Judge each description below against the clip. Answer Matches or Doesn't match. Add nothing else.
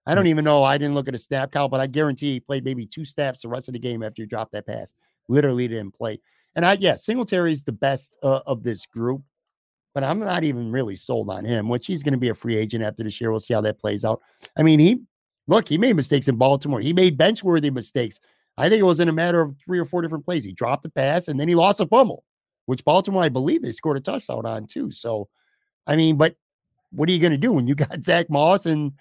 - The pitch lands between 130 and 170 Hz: Matches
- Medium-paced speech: Doesn't match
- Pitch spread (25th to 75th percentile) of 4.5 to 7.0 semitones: Matches